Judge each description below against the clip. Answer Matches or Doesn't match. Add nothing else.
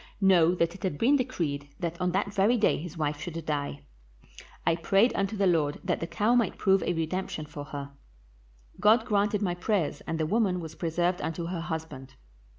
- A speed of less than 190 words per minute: Doesn't match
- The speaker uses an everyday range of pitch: Matches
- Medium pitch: Matches